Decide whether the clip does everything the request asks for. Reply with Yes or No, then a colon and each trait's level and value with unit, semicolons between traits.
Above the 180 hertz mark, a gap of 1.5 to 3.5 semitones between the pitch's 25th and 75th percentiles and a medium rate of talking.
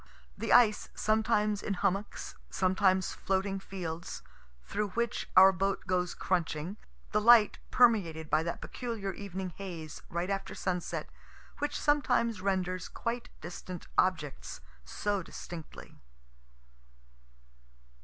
No: high, 190 Hz; average, 3.0 semitones; slow, 110 wpm